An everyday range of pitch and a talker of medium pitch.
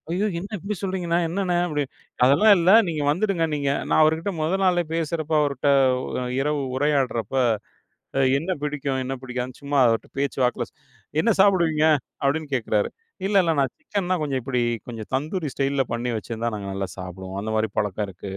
No: wide, 5.7 semitones; medium, 145 Hz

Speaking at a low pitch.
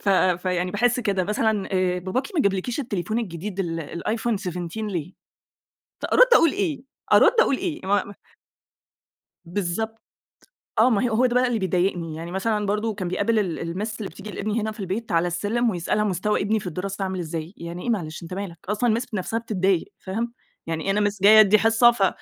No: high, 200 Hz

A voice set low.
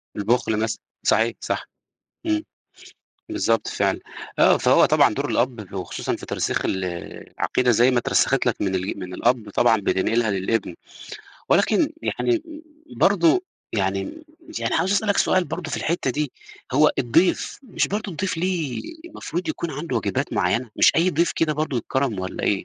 Yes: low, 130 Hz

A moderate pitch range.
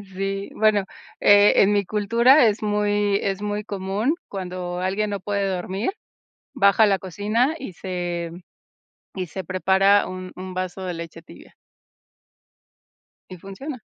No: narrow, 2.0 semitones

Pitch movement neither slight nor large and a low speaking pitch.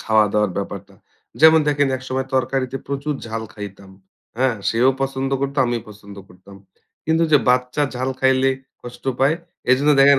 Yes: average, 3.4 semitones; low, 130 Hz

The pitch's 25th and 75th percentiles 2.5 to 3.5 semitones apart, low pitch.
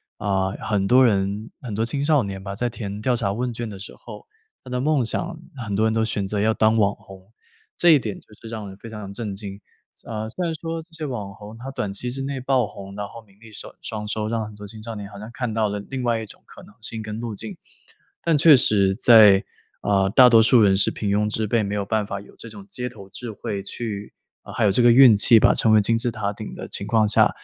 Yes: average, 2.8 semitones; low, 110 Hz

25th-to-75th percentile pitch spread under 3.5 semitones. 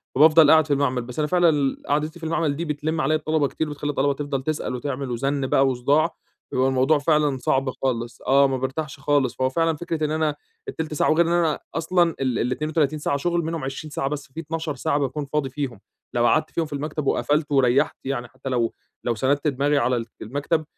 Yes: average, 2.8 semitones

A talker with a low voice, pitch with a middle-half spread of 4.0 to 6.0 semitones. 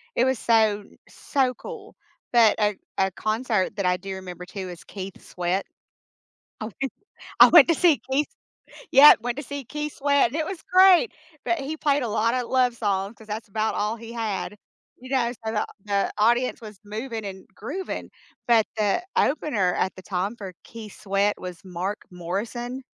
No: high, 220 Hz; average, 4.8 semitones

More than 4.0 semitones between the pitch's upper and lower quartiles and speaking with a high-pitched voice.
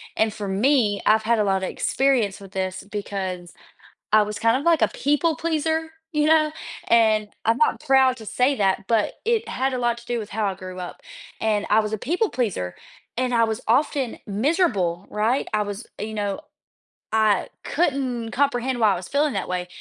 Yes: average, 4.8 semitones; high, 225 Hz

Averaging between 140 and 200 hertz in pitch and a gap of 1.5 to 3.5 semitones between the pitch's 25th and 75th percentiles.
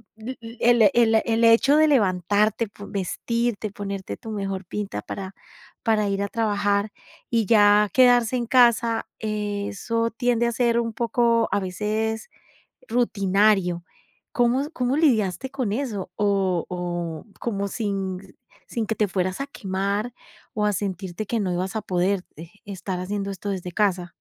No: high, 210 Hz; average, 3.1 semitones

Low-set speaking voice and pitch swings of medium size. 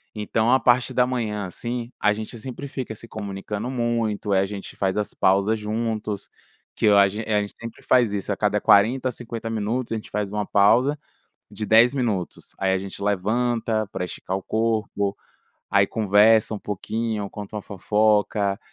No: low, 110 Hz; narrow, 2.3 semitones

